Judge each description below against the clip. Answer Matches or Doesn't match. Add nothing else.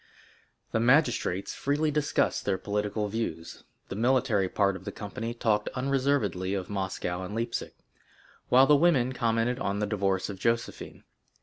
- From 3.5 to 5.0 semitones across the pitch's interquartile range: Matches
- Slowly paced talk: Doesn't match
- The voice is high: Doesn't match